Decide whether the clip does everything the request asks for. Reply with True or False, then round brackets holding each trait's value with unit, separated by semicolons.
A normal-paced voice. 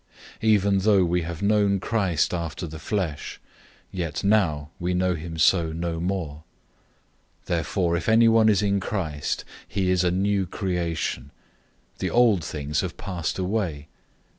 True (145 wpm)